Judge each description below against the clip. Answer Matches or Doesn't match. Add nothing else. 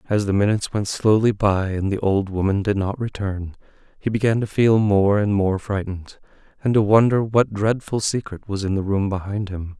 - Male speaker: Matches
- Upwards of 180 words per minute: Matches